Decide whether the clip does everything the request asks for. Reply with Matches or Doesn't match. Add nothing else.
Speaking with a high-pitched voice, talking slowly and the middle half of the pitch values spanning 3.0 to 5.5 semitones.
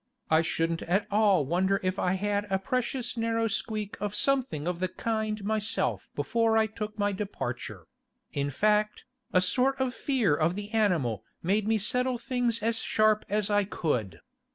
Doesn't match